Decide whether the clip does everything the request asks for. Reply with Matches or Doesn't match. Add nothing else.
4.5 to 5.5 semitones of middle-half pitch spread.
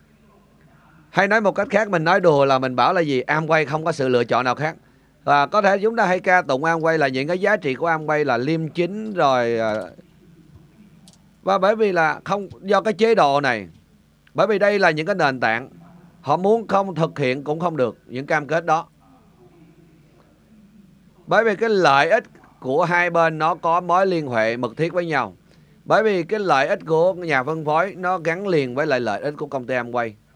Doesn't match